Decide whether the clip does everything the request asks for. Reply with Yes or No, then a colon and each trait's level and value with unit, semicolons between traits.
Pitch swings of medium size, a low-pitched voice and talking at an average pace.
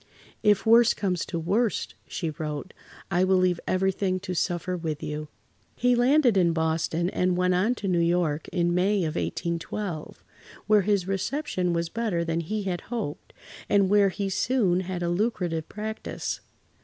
No: average, 3.4 semitones; medium, 185 Hz; average, 165 wpm